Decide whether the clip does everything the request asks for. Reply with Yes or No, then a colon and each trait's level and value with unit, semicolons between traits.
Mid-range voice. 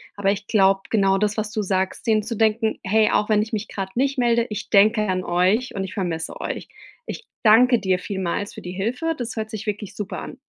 No: high, 210 Hz